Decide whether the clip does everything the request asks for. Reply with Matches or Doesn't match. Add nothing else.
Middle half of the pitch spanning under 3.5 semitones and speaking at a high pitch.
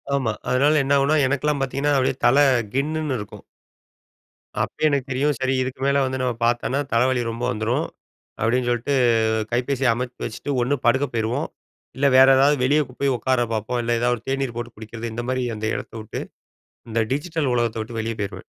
Doesn't match